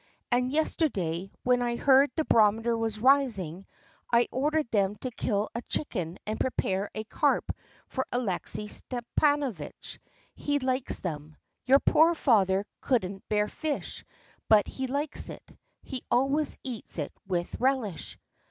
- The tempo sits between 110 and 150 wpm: Yes, slow, 135 wpm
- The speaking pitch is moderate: No, high, 235 Hz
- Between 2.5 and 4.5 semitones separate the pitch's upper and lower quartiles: No, average, 5.2 semitones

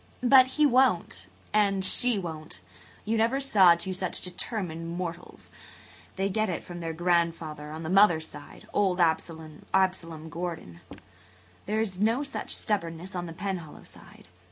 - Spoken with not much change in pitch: No, average, 4.0 semitones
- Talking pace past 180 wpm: No, average, 140 wpm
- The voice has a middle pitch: Yes, medium, 180 Hz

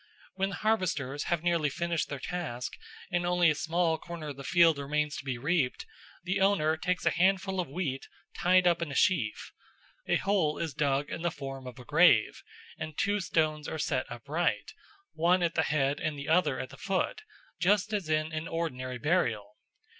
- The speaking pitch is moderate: Yes, medium, 160 Hz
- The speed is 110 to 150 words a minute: No, average, 190 wpm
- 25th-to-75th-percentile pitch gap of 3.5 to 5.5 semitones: Yes, average, 4.0 semitones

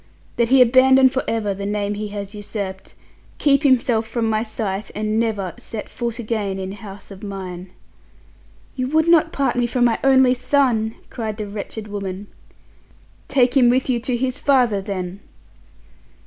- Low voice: No, high, 225 Hz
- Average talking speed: Yes, average, 165 wpm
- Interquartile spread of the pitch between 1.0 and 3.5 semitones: No, average, 3.9 semitones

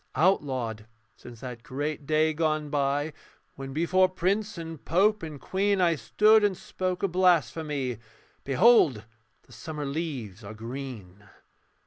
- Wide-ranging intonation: Yes, wide, 5.8 semitones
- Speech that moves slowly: Yes, slow, 130 wpm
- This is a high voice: No, medium, 150 Hz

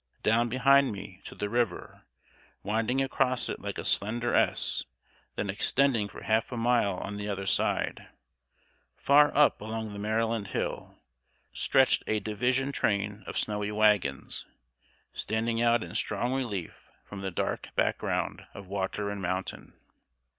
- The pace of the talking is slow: No, average, 145 wpm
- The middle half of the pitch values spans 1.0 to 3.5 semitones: Yes, average, 2.9 semitones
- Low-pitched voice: Yes, low, 110 Hz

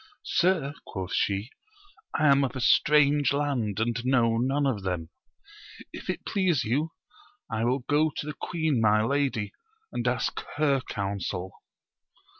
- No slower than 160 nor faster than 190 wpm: No, average, 145 wpm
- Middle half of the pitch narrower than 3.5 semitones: No, average, 5.1 semitones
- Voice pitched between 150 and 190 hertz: No, low, 130 Hz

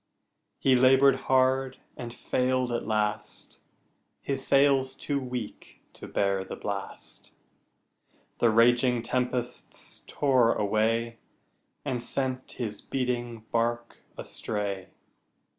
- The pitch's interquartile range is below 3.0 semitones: Yes, narrow, 2.5 semitones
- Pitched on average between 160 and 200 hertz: No, low, 120 Hz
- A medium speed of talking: No, slow, 100 wpm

